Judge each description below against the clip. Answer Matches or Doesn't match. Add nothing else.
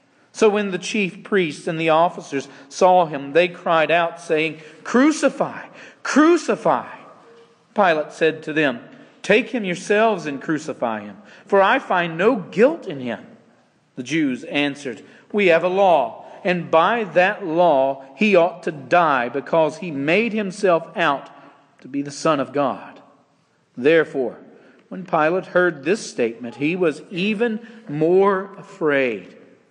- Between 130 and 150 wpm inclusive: Matches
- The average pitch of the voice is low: Doesn't match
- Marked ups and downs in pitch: Matches